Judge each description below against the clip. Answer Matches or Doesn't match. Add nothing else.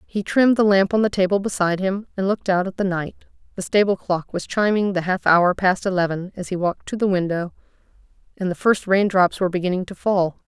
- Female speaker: Matches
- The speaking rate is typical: Doesn't match